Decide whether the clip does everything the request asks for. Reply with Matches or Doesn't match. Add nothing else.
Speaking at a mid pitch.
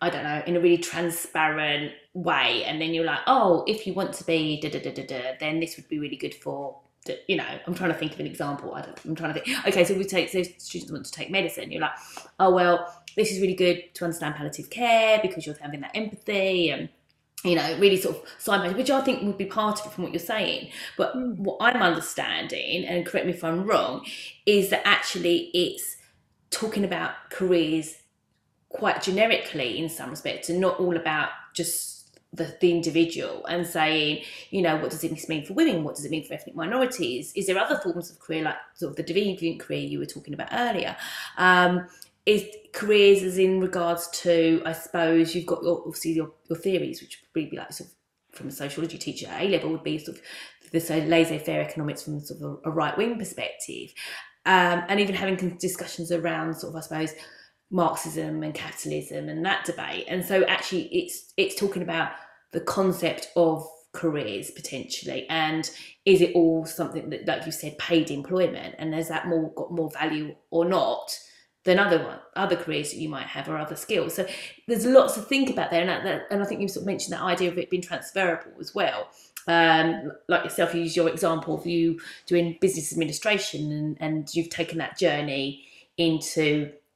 Matches